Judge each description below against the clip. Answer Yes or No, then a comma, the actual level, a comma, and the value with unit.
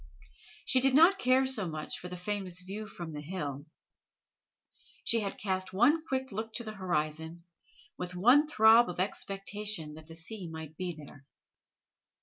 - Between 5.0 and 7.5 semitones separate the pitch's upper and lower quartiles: Yes, wide, 5.5 semitones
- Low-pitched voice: No, high, 190 Hz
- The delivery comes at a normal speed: Yes, average, 160 wpm